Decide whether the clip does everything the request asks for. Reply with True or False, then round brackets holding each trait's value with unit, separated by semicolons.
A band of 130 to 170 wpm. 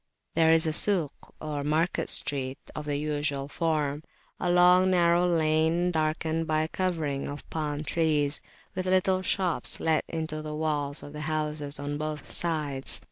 True (160 wpm)